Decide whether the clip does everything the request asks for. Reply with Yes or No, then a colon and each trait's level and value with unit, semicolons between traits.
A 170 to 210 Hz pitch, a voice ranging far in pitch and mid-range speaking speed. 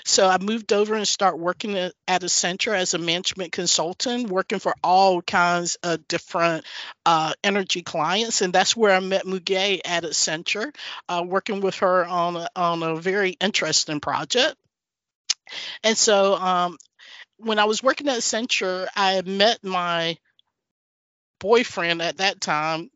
No: medium, 185 Hz; average, 2.8 semitones; average, 155 wpm